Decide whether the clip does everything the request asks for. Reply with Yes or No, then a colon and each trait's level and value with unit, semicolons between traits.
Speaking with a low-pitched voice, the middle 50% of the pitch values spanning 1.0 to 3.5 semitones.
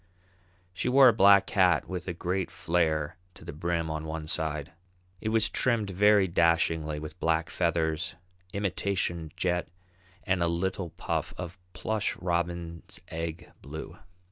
Yes: very low, 85 Hz; average, 2.8 semitones